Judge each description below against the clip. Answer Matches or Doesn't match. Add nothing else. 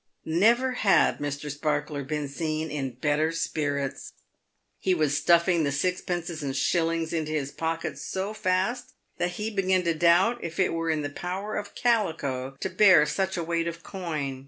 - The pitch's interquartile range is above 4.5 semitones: Doesn't match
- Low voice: Doesn't match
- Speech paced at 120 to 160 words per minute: Doesn't match